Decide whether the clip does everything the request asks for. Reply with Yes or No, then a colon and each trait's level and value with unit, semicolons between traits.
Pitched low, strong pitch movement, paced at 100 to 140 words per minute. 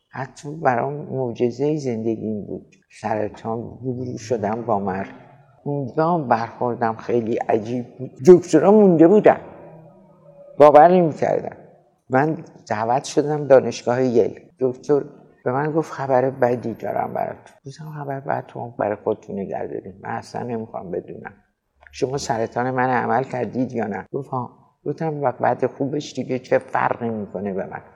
No: low, 130 Hz; average, 3.8 semitones; average, 130 wpm